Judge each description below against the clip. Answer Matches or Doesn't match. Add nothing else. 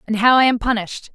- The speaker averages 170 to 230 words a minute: Doesn't match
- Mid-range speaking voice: Doesn't match